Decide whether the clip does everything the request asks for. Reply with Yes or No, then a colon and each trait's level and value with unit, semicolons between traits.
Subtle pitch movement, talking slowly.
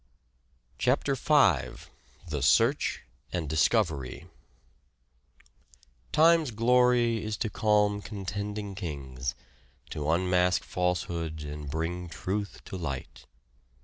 No: wide, 5.5 semitones; slow, 95 wpm